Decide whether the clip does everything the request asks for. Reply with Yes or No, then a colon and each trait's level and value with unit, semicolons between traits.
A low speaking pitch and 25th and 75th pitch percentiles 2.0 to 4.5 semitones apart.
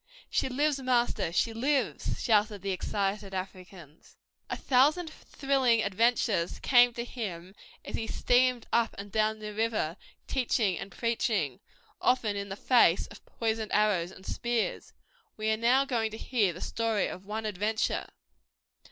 No: high, 220 Hz; average, 3.6 semitones